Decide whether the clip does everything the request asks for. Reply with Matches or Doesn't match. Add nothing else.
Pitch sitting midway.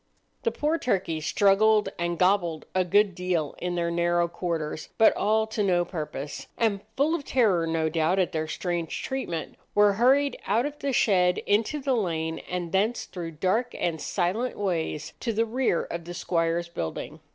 Matches